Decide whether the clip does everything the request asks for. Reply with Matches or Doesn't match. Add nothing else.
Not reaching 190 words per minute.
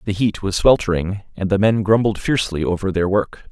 Doesn't match